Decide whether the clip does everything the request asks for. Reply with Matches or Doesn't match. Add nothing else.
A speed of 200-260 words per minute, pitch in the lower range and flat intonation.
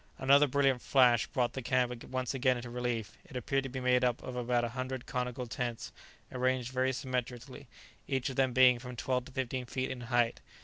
Matches